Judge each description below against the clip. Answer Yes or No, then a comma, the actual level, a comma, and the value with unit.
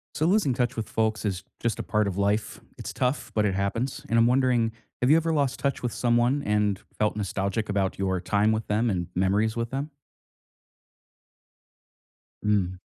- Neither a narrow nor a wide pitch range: Yes, average, 3.7 semitones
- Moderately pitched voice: No, low, 110 Hz